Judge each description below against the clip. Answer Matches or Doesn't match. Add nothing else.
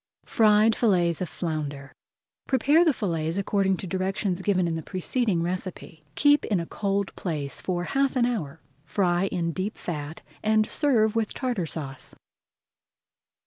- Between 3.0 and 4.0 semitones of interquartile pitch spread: Doesn't match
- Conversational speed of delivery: Matches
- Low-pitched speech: Doesn't match